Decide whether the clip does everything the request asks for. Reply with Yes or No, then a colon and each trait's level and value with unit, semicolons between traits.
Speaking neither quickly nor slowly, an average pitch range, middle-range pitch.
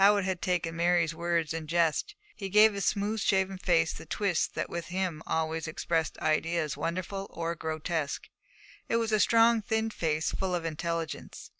Yes: average, 170 wpm; average, 3.4 semitones; medium, 170 Hz